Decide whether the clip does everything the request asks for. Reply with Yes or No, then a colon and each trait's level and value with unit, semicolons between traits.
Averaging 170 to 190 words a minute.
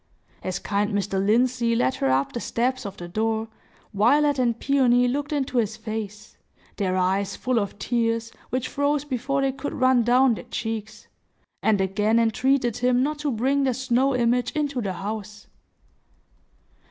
No: average, 155 wpm